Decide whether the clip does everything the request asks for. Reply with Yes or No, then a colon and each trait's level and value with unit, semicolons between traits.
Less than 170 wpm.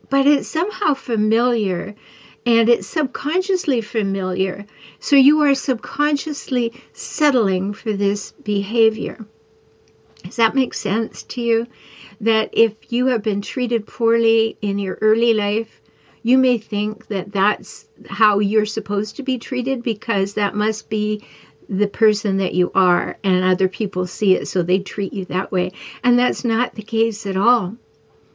Yes: average, 150 wpm